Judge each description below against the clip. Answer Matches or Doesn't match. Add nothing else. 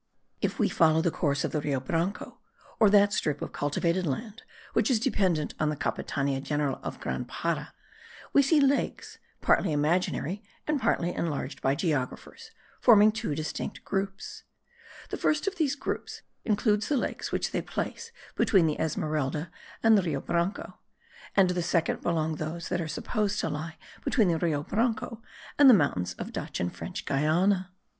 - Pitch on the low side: Doesn't match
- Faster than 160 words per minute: Matches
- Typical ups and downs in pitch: Doesn't match